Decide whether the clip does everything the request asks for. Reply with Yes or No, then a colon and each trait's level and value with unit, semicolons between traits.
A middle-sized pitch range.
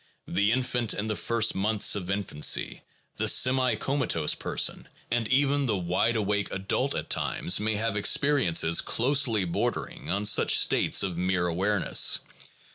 Yes: average, 4.2 semitones